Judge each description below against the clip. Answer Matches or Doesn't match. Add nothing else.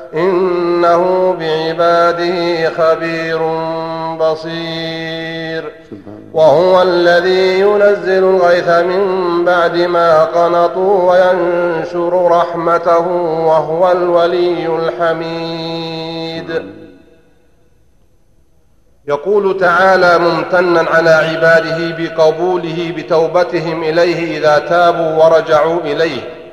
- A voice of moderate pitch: Matches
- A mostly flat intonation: Matches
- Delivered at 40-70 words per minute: Matches